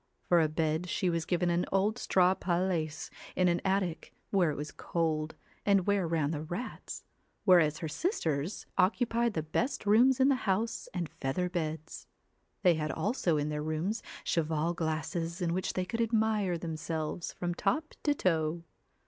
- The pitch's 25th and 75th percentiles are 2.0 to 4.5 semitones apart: Yes, average, 3.8 semitones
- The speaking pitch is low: No, medium, 175 Hz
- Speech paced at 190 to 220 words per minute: No, average, 175 wpm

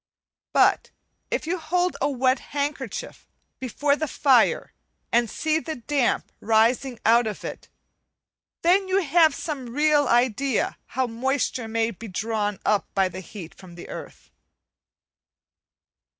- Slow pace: Yes, slow, 130 wpm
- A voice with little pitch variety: No, average, 4.8 semitones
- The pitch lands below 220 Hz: No, very high, 255 Hz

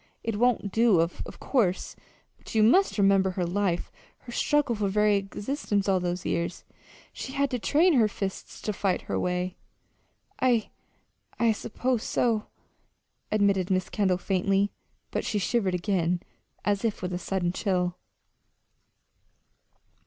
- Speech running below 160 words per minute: Yes, average, 140 wpm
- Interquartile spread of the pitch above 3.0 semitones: Yes, average, 3.6 semitones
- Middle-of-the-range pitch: No, high, 200 Hz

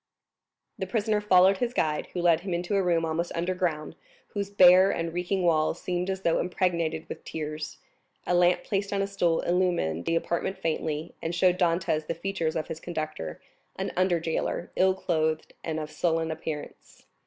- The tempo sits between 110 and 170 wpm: No, average, 180 wpm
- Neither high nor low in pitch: Yes, medium, 175 Hz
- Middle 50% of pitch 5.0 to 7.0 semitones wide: No, narrow, 2.6 semitones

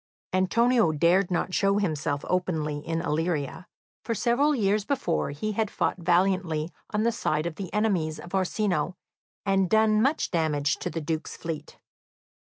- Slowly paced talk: No, average, 155 wpm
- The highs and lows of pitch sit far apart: No, average, 4.6 semitones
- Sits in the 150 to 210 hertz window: Yes, medium, 185 Hz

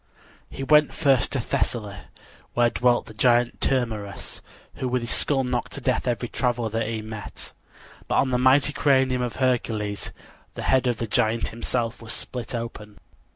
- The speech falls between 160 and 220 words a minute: Yes, average, 170 wpm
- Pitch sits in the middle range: No, low, 120 Hz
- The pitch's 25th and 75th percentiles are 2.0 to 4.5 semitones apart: Yes, narrow, 2.4 semitones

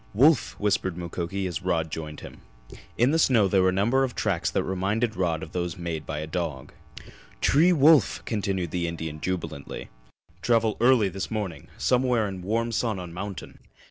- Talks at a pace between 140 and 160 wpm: No, average, 175 wpm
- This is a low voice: Yes, very low, 95 Hz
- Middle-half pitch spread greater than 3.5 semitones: Yes, average, 5.0 semitones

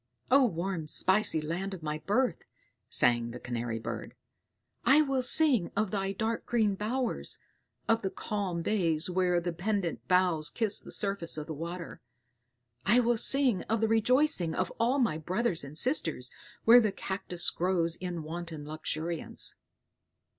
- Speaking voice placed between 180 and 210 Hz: Yes, medium, 185 Hz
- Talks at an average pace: Yes, average, 155 wpm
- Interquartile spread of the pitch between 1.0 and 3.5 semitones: No, wide, 5.4 semitones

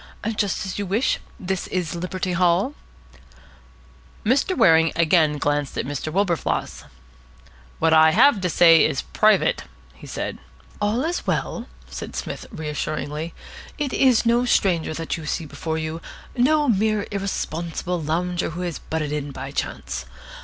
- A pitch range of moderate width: Yes, average, 4.6 semitones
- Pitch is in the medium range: Yes, medium, 175 Hz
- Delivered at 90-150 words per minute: Yes, average, 145 wpm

